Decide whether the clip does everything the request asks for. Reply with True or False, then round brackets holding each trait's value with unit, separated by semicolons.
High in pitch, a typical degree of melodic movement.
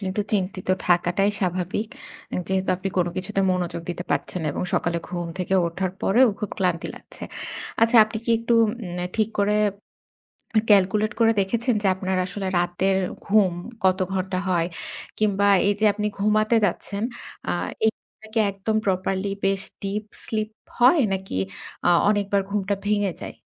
False (195 Hz; 2.3 semitones)